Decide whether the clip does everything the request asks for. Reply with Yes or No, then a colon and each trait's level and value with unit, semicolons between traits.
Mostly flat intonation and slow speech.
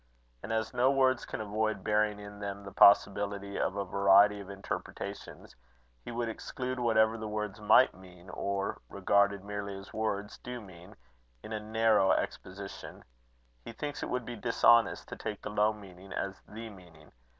No: narrow, 2.1 semitones; average, 170 wpm